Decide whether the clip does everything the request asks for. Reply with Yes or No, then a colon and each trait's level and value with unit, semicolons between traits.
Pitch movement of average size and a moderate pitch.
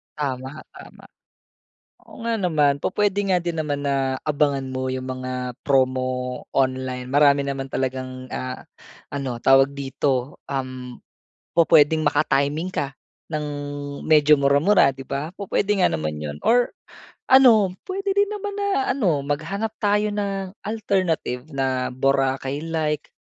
No: wide, 6.1 semitones; medium, 145 Hz